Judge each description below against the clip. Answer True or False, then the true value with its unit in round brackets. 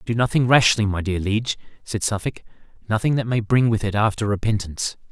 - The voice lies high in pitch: False (110 Hz)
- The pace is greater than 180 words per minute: True (190 wpm)